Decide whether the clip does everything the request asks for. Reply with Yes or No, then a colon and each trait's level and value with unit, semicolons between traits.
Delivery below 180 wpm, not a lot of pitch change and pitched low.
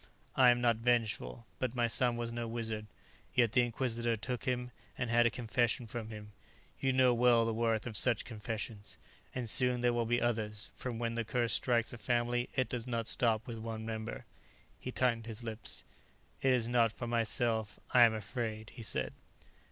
No: average, 190 wpm; narrow, 1.5 semitones; low, 115 Hz